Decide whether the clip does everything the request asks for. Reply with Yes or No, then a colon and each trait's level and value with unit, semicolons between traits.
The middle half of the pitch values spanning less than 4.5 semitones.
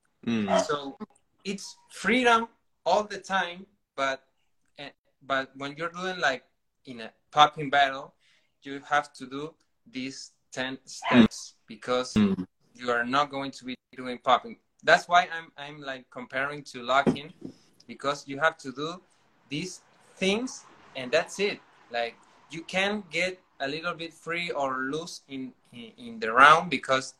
No: wide, 5.6 semitones